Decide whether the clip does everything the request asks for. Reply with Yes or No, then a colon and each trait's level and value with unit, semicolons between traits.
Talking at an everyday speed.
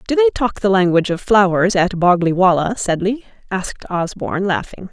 Yes: average, 170 wpm